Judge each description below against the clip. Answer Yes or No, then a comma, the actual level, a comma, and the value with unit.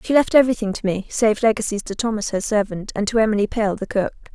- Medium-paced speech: No, fast, 235 wpm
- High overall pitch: Yes, high, 215 Hz